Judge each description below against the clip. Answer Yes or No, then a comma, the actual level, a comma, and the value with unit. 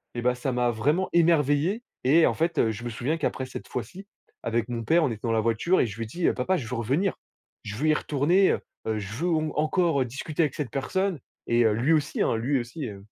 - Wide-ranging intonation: Yes, wide, 5.7 semitones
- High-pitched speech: No, low, 135 Hz